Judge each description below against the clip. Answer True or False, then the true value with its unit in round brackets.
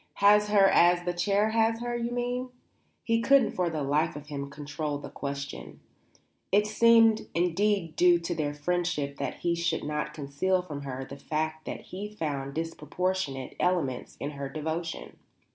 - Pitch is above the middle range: False (170 Hz)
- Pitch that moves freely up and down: True (5.7 semitones)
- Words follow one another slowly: False (165 wpm)